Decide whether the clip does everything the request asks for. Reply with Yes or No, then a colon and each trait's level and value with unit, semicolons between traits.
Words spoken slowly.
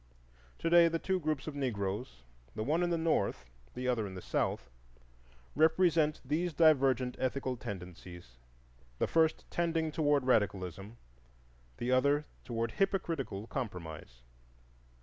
Yes: slow, 130 wpm